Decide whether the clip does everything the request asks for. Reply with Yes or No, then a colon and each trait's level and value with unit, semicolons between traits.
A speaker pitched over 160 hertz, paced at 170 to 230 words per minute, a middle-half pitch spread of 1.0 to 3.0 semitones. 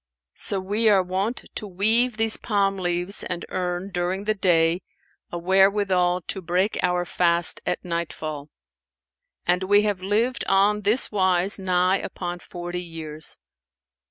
No: medium, 185 Hz; average, 140 wpm; narrow, 2.4 semitones